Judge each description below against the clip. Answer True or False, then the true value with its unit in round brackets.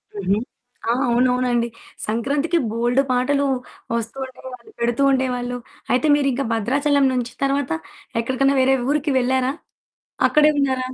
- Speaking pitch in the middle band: False (255 Hz)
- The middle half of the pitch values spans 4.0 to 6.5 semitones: False (2.4 semitones)